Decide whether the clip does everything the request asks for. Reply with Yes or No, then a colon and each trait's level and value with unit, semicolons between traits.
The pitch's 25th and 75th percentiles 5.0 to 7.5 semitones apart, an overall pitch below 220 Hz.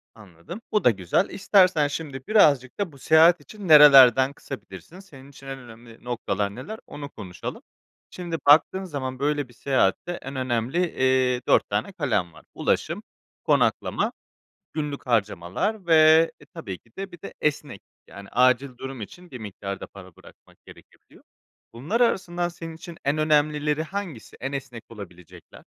Yes: wide, 5.5 semitones; medium, 140 Hz